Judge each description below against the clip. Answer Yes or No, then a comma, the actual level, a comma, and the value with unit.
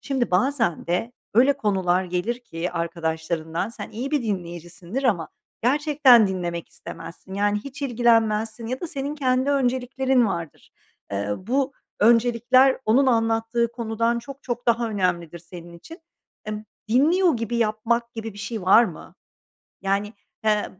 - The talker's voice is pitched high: Yes, high, 225 Hz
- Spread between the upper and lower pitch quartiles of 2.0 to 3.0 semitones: No, average, 5.3 semitones